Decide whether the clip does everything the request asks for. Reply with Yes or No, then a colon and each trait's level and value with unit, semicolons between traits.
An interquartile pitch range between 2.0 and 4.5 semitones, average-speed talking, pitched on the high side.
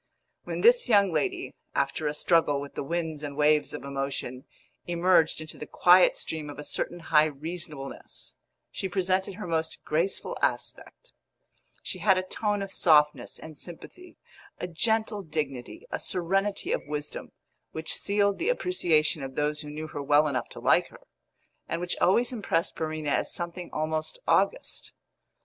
No: average, 3.8 semitones; average, 160 wpm; medium, 160 Hz